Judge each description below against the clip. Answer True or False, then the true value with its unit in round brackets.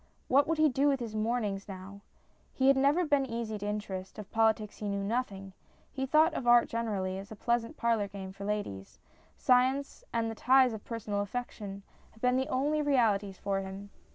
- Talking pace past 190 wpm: True (200 wpm)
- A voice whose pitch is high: True (225 Hz)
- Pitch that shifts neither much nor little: True (4.3 semitones)